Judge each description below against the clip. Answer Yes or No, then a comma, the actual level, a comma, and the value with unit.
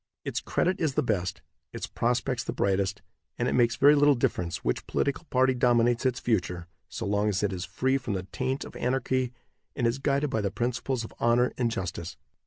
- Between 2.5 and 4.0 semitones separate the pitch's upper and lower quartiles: No, average, 4.5 semitones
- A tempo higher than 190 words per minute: Yes, average, 200 wpm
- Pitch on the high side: No, low, 120 Hz